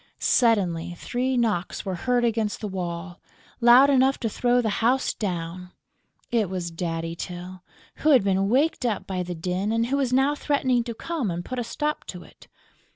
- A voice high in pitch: Yes, high, 220 Hz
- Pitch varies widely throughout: Yes, wide, 5.7 semitones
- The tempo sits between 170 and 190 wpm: Yes, average, 185 wpm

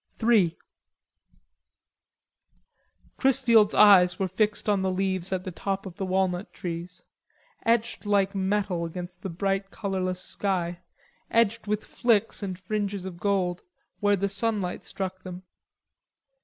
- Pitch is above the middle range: Yes, high, 195 Hz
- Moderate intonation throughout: No, narrow, 2.1 semitones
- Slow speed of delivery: Yes, slow, 130 wpm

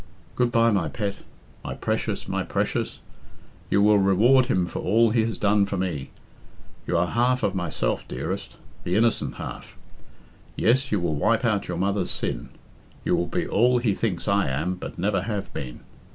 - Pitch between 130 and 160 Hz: No, low, 100 Hz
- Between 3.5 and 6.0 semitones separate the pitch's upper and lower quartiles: Yes, average, 4.2 semitones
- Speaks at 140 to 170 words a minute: No, average, 180 wpm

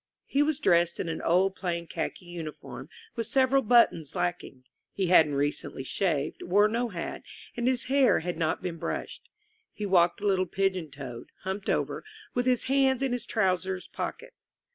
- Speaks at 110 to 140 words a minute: No, average, 170 wpm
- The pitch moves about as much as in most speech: No, wide, 6.1 semitones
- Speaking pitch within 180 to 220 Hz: Yes, high, 190 Hz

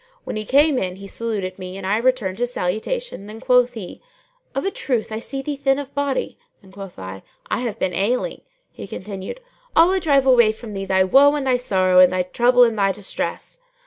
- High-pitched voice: Yes, high, 225 Hz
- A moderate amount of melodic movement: No, wide, 5.8 semitones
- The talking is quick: Yes, fast, 215 wpm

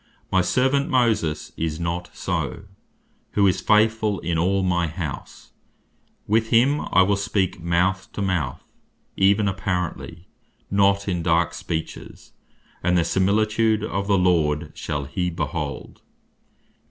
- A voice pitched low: Yes, very low, 95 Hz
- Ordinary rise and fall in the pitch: Yes, average, 3.2 semitones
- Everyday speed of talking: No, slow, 130 wpm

